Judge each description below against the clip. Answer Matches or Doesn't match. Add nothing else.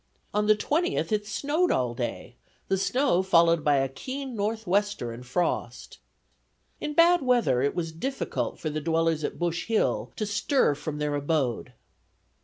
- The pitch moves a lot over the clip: Matches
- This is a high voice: Doesn't match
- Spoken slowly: Doesn't match